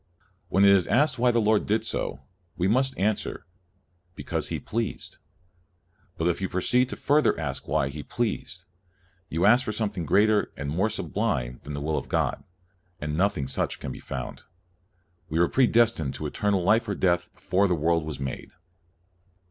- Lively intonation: Yes, wide, 5.8 semitones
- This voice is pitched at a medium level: No, very low, 95 Hz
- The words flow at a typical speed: Yes, average, 180 wpm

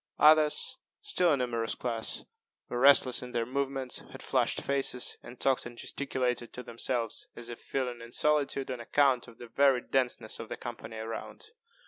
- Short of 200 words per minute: Yes, average, 170 wpm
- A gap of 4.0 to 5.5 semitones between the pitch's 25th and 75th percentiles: No, average, 2.7 semitones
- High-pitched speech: No, low, 125 Hz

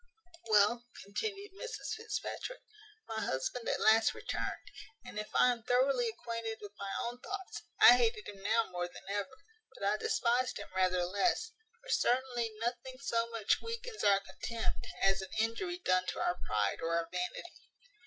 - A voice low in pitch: No, high, 230 Hz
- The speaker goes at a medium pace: Yes, average, 165 wpm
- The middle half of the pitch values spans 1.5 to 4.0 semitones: No, average, 4.8 semitones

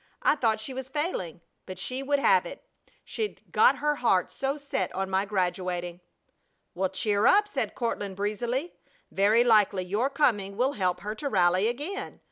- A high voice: Yes, high, 220 Hz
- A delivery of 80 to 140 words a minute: No, average, 170 wpm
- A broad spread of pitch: Yes, wide, 6.6 semitones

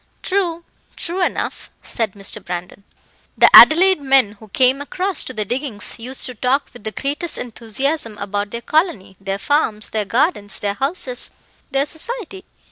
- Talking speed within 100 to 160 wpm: Yes, average, 155 wpm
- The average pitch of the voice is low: No, very high, 255 Hz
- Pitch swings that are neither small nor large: No, wide, 6.8 semitones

